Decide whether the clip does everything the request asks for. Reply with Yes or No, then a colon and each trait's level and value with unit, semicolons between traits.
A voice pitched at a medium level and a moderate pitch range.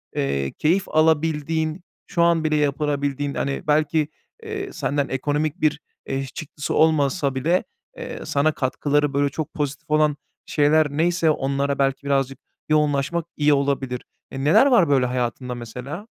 No: medium, 145 Hz; narrow, 2.2 semitones